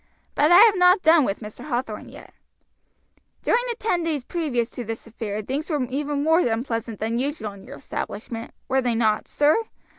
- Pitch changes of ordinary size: No, wide, 5.9 semitones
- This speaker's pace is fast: No, average, 185 wpm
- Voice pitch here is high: Yes, very high, 260 Hz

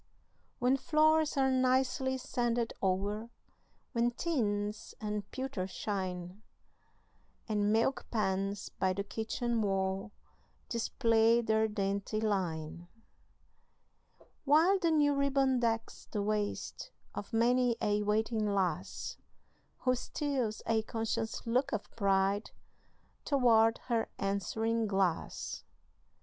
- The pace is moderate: No, slow, 105 wpm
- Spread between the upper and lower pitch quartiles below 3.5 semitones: No, average, 3.9 semitones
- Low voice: No, high, 225 Hz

